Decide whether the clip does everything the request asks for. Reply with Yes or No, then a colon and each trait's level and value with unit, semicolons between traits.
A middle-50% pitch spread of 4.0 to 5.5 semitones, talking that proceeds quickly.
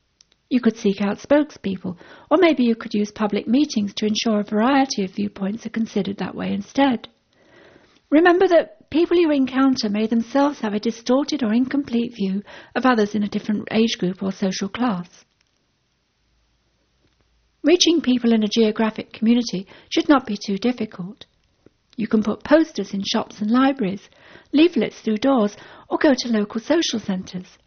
No: average, 4.6 semitones; average, 160 wpm